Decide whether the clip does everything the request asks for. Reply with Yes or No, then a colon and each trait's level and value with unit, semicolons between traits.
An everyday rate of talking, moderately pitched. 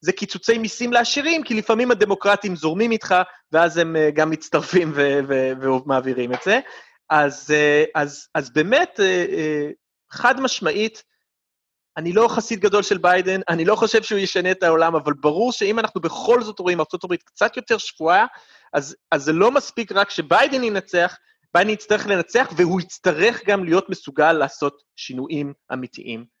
No: fast, 165 wpm; medium, 180 Hz